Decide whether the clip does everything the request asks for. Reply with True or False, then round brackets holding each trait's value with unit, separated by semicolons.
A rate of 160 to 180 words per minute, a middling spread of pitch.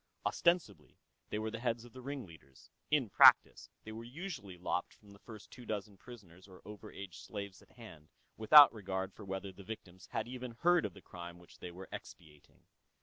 False (195 wpm; 4.3 semitones)